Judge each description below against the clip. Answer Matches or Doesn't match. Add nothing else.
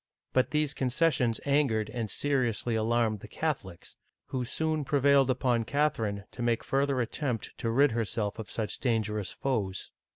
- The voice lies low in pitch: Matches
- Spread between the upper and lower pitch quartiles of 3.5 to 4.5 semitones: Matches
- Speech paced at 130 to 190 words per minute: Matches